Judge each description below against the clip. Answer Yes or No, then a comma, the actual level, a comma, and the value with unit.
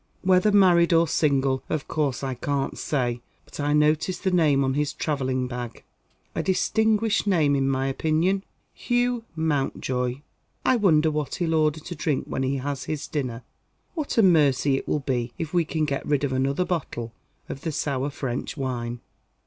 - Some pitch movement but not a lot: Yes, average, 4.1 semitones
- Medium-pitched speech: Yes, medium, 145 Hz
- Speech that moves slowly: No, average, 175 wpm